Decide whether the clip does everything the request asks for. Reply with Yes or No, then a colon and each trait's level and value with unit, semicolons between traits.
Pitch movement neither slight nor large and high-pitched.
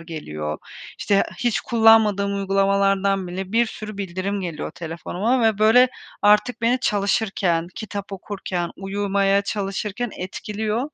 No: narrow, 2.2 semitones; high, 200 Hz